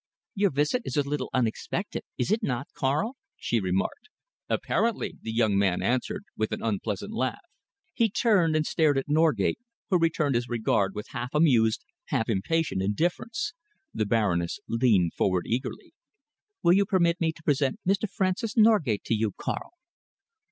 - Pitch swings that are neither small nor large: No, wide, 8.1 semitones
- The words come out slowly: No, average, 160 wpm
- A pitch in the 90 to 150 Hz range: Yes, medium, 140 Hz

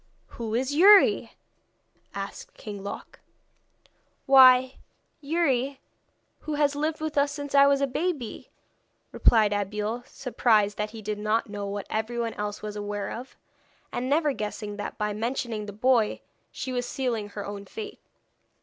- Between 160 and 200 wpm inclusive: No, average, 150 wpm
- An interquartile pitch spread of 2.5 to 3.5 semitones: No, average, 4.9 semitones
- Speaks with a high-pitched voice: Yes, high, 235 Hz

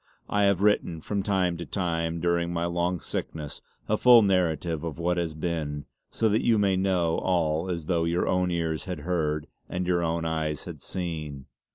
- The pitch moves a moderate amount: No, narrow, 2.0 semitones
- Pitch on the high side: No, very low, 85 Hz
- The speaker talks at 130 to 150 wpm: No, average, 190 wpm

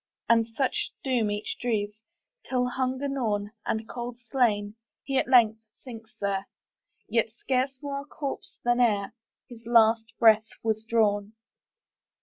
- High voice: Yes, high, 230 Hz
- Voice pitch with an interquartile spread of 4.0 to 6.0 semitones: No, narrow, 2.6 semitones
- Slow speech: Yes, slow, 120 wpm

